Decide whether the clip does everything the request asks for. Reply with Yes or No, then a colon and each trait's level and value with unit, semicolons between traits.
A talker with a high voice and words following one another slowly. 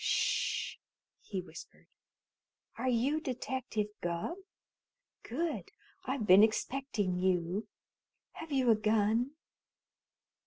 Yes: high, 225 Hz; slow, 90 wpm